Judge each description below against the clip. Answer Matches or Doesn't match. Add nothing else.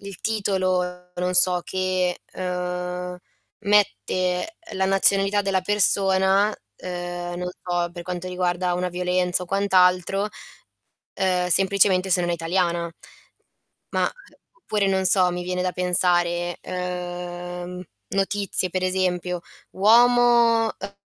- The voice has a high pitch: Doesn't match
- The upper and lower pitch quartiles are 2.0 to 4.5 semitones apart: Doesn't match